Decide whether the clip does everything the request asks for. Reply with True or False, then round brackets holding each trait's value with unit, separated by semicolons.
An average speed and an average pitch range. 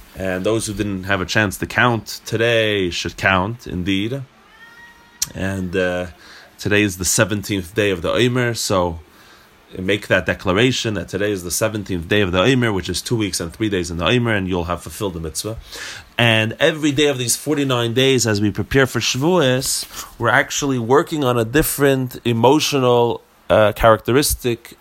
True (175 wpm; 4.7 semitones)